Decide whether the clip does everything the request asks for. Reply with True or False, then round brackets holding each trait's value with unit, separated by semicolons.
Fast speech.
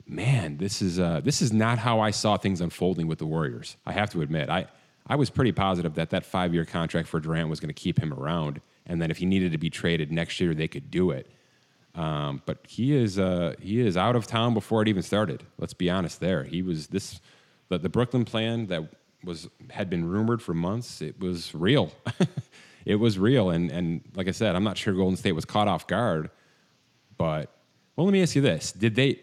True (230 wpm)